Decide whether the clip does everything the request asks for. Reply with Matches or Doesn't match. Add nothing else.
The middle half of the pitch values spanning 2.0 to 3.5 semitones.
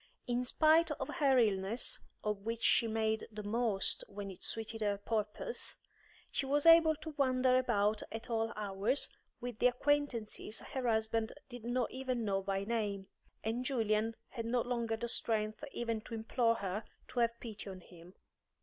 Matches